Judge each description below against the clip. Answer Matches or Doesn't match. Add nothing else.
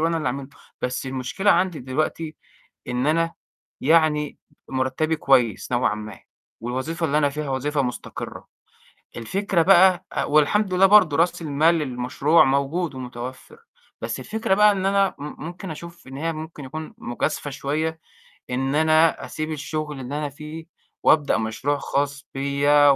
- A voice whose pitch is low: Doesn't match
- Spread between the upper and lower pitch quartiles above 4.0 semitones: Doesn't match